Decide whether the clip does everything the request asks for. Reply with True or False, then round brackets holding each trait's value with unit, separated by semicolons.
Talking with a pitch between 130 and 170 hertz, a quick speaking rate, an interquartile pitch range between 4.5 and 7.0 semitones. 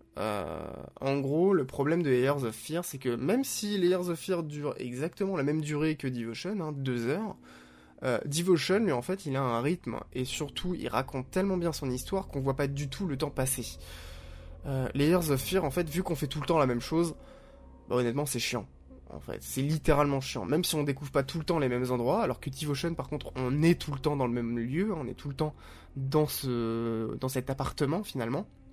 True (140 Hz; 230 wpm; 4.8 semitones)